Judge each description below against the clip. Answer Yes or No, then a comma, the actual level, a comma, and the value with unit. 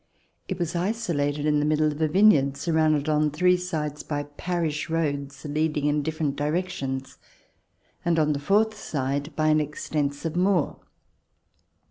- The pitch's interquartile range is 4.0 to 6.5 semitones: No, narrow, 2.5 semitones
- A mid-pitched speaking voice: Yes, medium, 150 Hz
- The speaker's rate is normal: Yes, average, 145 wpm